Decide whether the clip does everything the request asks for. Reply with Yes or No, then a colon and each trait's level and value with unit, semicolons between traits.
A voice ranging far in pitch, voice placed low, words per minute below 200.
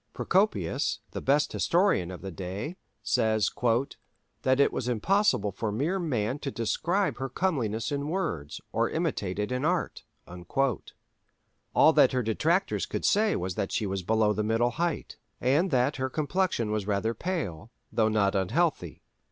Yes: wide, 7.5 semitones; low, 120 Hz; average, 155 wpm